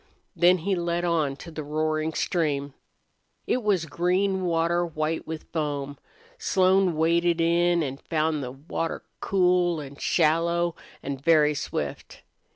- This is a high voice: No, medium, 165 Hz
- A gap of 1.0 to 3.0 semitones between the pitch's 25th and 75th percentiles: Yes, narrow, 2.4 semitones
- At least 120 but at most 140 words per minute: Yes, slow, 135 wpm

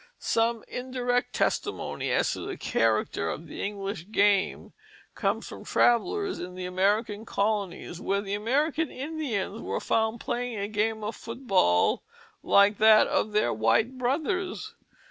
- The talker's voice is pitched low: No, high, 220 Hz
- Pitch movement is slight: No, average, 3.8 semitones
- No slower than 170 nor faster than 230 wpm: No, average, 145 wpm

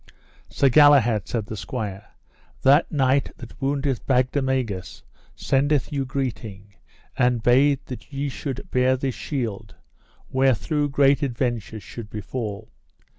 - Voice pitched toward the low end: Yes, low, 130 Hz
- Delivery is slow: Yes, slow, 120 wpm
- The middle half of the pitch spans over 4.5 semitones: No, average, 3.6 semitones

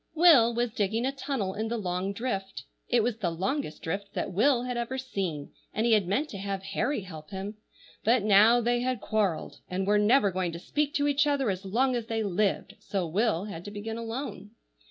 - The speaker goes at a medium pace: No, fast, 215 wpm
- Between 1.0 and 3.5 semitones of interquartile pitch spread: No, average, 4.0 semitones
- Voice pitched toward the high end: Yes, high, 215 Hz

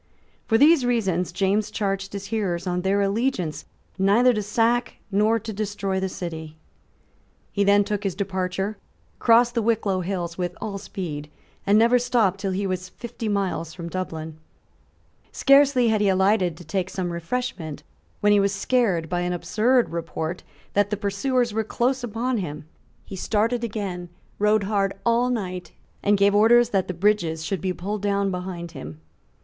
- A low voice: No, high, 200 Hz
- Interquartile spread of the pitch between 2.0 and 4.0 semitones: Yes, average, 3.6 semitones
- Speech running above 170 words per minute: No, average, 165 wpm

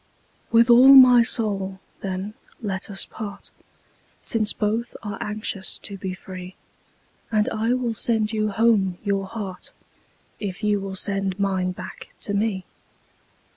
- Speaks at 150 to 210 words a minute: No, slow, 135 wpm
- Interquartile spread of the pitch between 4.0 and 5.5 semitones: No, average, 2.7 semitones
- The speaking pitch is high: Yes, high, 205 Hz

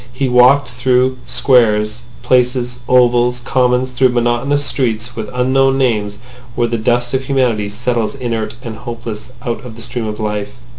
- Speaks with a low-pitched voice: Yes, low, 120 Hz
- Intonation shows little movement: Yes, narrow, 2.1 semitones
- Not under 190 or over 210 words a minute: No, average, 155 wpm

